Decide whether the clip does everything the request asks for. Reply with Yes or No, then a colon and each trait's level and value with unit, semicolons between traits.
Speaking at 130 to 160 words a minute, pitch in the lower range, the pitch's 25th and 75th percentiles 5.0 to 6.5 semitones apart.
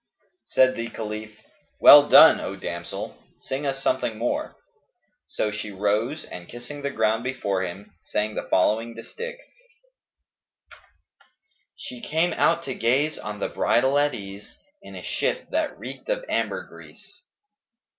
Yes: average, 145 wpm; low, 120 Hz; wide, 5.6 semitones